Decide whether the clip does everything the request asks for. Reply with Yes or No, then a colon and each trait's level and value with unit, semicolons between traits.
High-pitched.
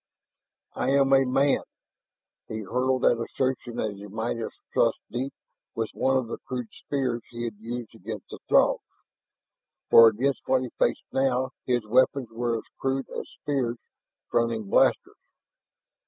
No: low, 120 Hz